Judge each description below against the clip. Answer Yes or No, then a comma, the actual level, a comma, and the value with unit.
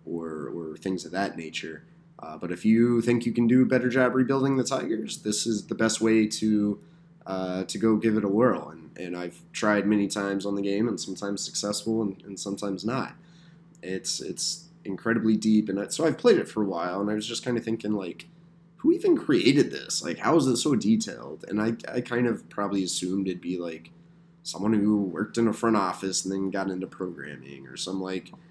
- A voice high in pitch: No, low, 105 Hz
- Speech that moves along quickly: Yes, fast, 220 wpm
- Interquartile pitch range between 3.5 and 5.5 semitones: Yes, average, 4.9 semitones